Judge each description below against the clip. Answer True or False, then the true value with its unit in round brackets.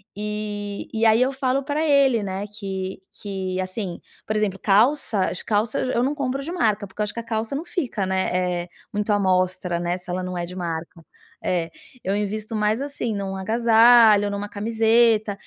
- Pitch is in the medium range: False (210 Hz)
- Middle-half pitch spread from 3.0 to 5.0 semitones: True (3.4 semitones)